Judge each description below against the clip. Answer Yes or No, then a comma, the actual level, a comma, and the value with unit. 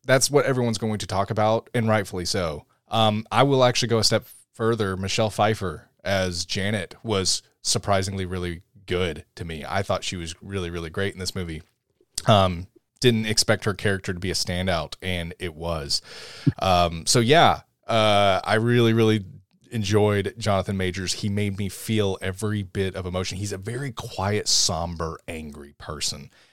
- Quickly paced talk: No, average, 170 wpm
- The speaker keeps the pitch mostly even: No, average, 3.4 semitones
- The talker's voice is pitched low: Yes, low, 100 Hz